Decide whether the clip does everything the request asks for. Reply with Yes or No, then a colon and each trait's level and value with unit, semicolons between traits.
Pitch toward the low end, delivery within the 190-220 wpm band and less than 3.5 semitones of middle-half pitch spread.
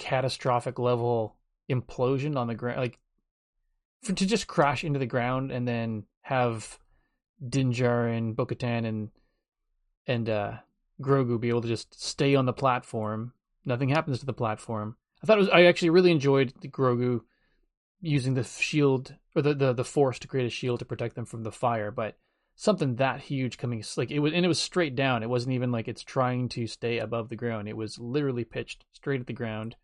Yes: low, 125 Hz; average, 195 wpm; average, 2.9 semitones